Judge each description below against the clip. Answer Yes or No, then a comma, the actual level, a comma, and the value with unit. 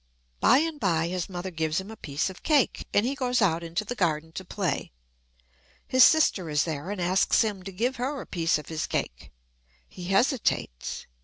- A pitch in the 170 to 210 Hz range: Yes, medium, 185 Hz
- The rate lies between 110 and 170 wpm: No, average, 200 wpm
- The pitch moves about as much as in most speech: No, wide, 6.6 semitones